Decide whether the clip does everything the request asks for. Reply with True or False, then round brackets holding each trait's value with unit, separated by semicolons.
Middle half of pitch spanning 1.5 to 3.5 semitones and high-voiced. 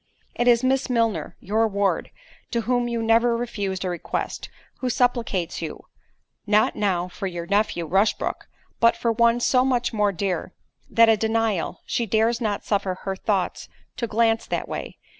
True (3.0 semitones; 225 Hz)